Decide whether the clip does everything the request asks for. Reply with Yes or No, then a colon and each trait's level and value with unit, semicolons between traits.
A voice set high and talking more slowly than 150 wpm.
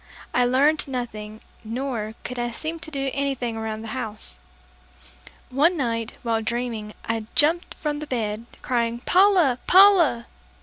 Yes: high, 245 Hz; average, 140 wpm